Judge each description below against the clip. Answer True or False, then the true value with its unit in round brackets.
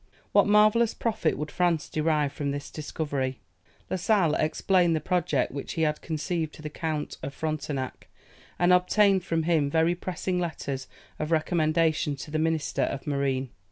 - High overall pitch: False (160 Hz)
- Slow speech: False (160 wpm)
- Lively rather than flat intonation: False (3.0 semitones)